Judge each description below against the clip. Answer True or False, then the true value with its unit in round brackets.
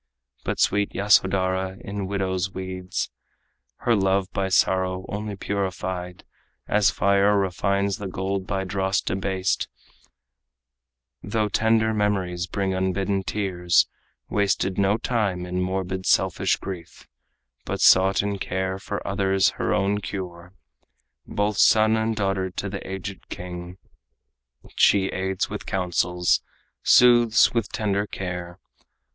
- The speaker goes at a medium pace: False (120 wpm)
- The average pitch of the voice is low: True (95 Hz)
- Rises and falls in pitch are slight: True (1.5 semitones)